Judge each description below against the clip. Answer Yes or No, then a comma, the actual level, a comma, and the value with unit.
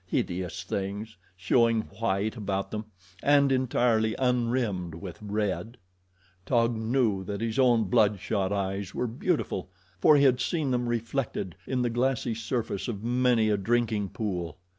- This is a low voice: Yes, low, 110 Hz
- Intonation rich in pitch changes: No, average, 3.7 semitones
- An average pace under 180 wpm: Yes, average, 145 wpm